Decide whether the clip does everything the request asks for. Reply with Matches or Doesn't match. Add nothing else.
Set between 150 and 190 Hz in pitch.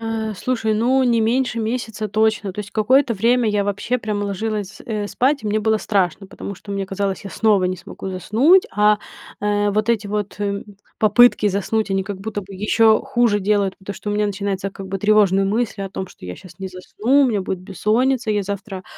Doesn't match